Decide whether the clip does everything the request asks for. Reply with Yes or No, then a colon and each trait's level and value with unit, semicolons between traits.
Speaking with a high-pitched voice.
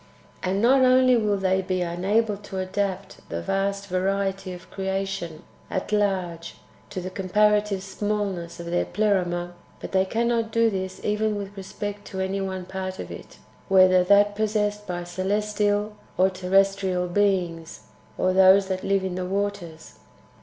Yes: high, 195 Hz